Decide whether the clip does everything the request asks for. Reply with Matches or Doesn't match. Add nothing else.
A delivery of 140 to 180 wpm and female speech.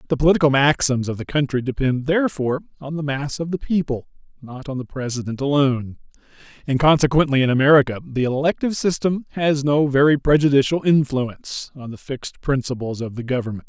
Doesn't match